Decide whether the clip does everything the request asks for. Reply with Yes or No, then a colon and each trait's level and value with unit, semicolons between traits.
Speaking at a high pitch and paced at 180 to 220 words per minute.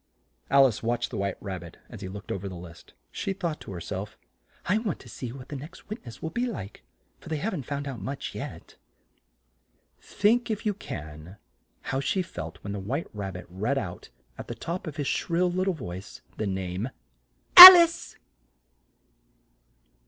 No: low, 135 Hz; average, 190 wpm